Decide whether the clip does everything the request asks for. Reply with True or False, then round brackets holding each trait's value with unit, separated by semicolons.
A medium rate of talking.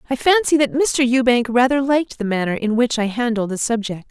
False (220 wpm)